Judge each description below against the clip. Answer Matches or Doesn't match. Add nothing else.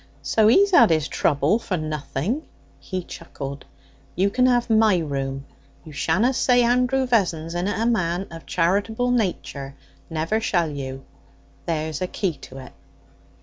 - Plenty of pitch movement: Matches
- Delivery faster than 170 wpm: Doesn't match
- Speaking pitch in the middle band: Matches